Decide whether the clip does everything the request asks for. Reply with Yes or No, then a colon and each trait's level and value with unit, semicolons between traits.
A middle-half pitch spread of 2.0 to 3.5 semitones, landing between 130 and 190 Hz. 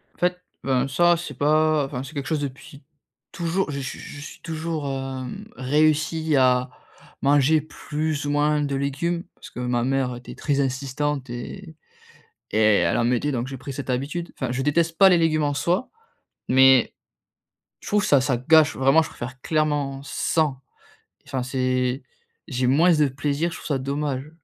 Yes: average, 3.1 semitones; medium, 140 Hz